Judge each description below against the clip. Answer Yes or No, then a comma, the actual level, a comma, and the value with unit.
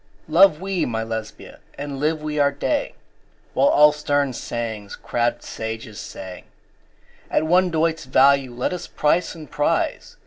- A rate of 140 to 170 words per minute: Yes, average, 145 wpm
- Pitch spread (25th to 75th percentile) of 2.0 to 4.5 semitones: No, average, 5.3 semitones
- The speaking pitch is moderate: Yes, medium, 145 Hz